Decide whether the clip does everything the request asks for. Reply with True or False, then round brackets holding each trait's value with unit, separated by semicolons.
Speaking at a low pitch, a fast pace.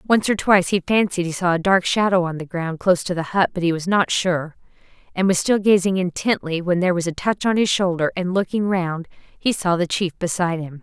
False (180 Hz; 245 wpm)